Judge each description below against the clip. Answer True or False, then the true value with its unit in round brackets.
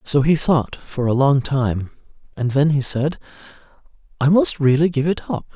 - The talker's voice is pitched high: False (140 Hz)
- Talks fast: False (185 wpm)